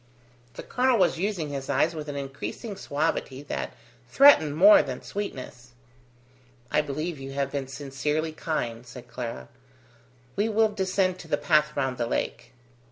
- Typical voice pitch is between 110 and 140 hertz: No, medium, 150 Hz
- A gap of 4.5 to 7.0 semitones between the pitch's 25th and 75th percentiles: Yes, average, 5.2 semitones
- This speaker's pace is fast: No, average, 155 wpm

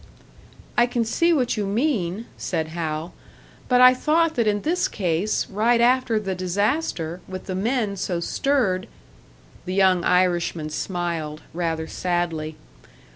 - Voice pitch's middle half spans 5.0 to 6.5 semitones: Yes, wide, 5.6 semitones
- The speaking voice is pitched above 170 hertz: Yes, high, 190 Hz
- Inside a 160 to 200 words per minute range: No, average, 140 wpm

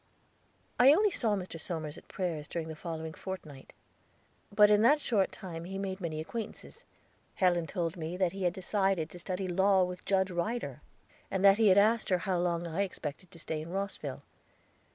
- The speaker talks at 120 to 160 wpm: No, average, 190 wpm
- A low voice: No, medium, 185 Hz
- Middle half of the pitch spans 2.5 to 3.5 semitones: Yes, average, 2.9 semitones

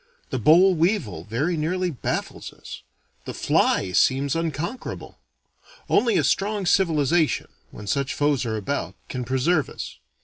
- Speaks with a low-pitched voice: No, medium, 155 Hz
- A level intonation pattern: No, wide, 5.5 semitones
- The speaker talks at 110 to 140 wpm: Yes, slow, 135 wpm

